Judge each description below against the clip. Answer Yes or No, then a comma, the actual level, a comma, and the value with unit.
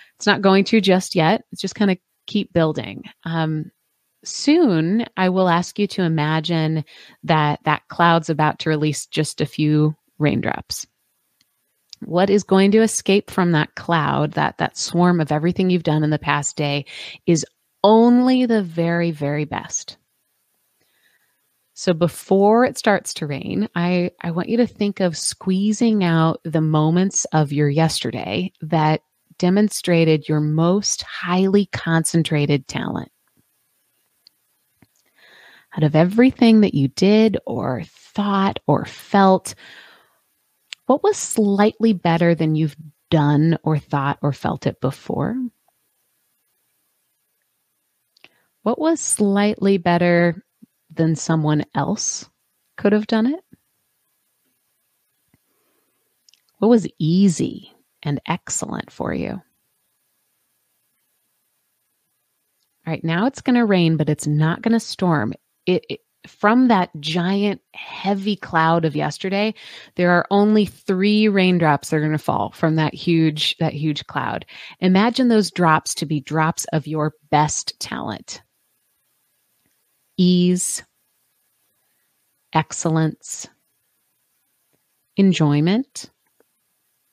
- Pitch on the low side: No, medium, 175 Hz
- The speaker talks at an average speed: No, slow, 120 wpm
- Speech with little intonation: No, average, 4.7 semitones